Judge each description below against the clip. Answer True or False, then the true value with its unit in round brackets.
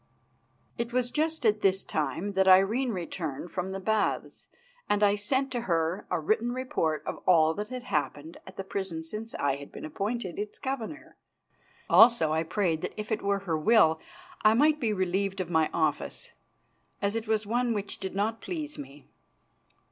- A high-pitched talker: True (200 Hz)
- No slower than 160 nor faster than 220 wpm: True (180 wpm)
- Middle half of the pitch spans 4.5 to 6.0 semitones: True (5.5 semitones)